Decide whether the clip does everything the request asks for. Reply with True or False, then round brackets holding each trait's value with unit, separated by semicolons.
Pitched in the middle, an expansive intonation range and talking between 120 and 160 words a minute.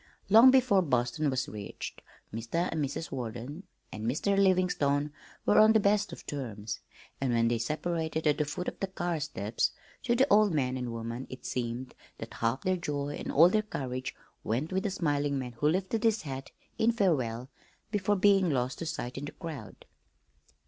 False (150 Hz; 6.9 semitones; 185 wpm)